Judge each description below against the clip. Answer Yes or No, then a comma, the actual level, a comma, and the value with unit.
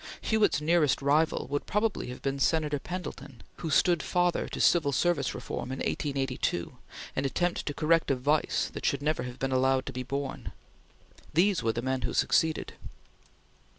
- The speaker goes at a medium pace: Yes, average, 170 wpm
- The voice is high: No, medium, 145 Hz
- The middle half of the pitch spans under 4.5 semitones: Yes, average, 3.9 semitones